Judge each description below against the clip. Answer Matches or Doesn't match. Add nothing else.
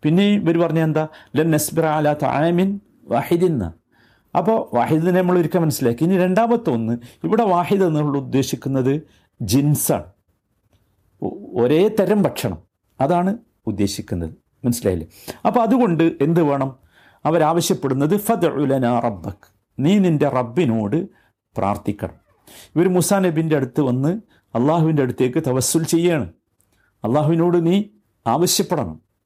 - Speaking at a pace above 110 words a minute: Doesn't match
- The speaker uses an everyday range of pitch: Doesn't match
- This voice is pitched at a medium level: Matches